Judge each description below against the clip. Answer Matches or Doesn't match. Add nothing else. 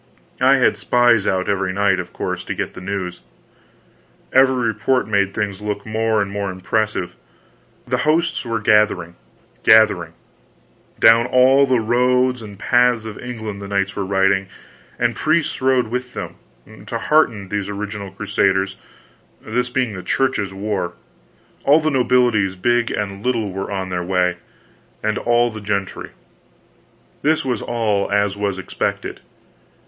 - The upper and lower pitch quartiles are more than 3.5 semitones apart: Matches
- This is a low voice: Matches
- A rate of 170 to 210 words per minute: Doesn't match